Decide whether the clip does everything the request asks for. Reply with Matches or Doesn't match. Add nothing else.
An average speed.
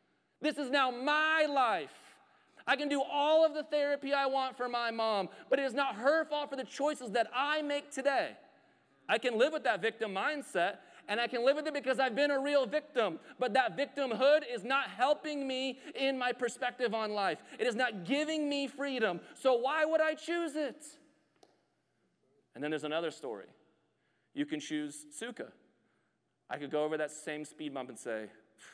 Matches